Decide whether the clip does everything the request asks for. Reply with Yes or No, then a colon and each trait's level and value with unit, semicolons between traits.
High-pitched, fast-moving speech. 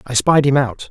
No: low, 135 Hz; fast, 265 wpm